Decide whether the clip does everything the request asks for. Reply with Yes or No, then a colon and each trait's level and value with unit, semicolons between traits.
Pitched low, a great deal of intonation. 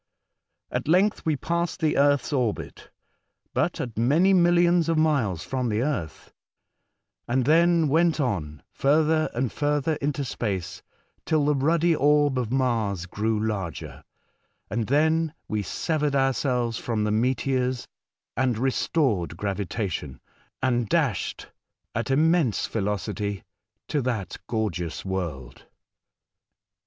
Yes: low, 130 Hz; wide, 6.3 semitones